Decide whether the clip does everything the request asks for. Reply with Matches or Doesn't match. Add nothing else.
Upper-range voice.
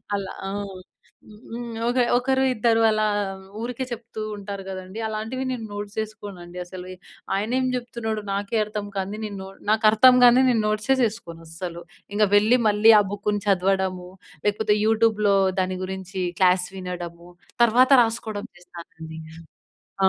Matches